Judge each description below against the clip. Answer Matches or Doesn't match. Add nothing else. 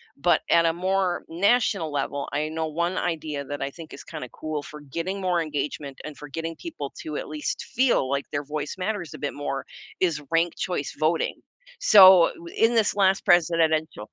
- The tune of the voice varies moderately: Matches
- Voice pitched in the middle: Matches